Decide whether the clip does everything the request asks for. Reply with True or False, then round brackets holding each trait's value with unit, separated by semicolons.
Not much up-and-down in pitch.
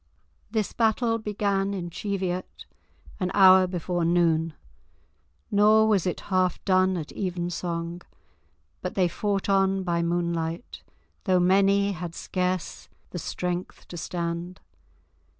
True (2.3 semitones)